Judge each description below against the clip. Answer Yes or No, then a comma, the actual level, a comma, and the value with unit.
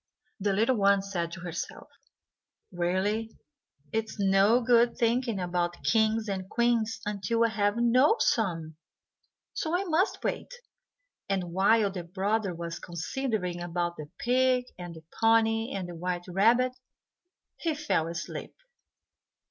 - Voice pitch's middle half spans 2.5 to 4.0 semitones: No, average, 4.7 semitones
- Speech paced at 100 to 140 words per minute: Yes, slow, 135 wpm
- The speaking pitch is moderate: No, high, 205 Hz